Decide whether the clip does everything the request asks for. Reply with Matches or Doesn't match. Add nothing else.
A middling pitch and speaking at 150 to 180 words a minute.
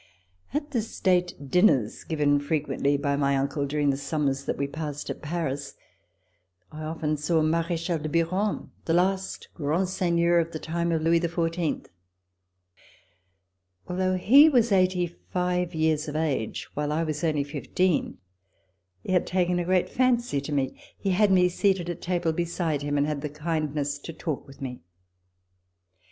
Matches